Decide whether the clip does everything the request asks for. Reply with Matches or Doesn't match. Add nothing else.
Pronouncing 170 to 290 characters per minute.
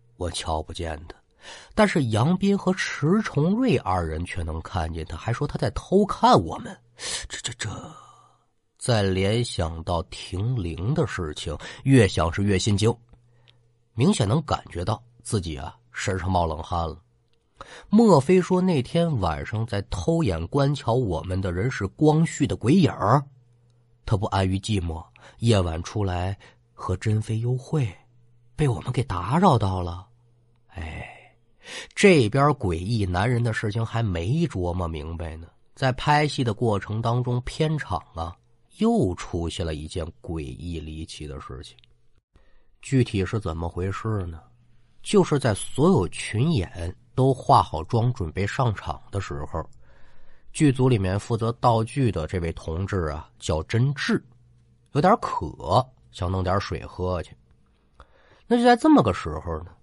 Matches